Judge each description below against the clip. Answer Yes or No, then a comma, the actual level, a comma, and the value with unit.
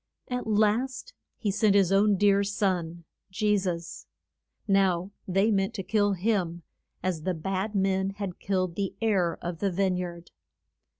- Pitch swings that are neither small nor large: No, narrow, 2.3 semitones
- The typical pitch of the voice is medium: No, high, 195 Hz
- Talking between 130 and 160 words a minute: Yes, average, 155 wpm